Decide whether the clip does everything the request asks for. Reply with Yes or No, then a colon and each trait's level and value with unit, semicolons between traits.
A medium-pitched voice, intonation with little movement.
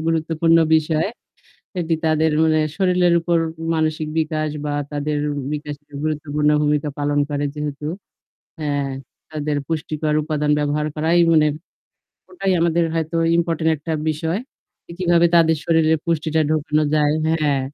Yes: medium, 155 Hz; narrow, 1.6 semitones